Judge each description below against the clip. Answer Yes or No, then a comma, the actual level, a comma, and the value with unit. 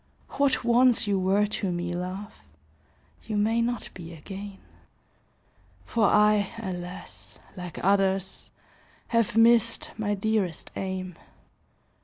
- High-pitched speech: Yes, high, 200 Hz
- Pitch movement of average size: Yes, average, 3.4 semitones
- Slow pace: Yes, slow, 110 wpm